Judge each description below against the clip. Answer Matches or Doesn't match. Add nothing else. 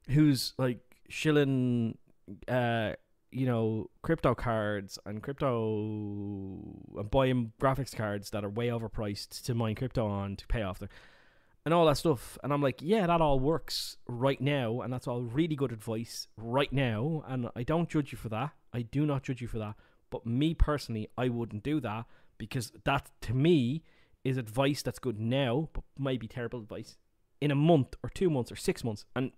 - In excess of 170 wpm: Matches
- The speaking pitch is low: Matches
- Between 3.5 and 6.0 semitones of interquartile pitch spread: Matches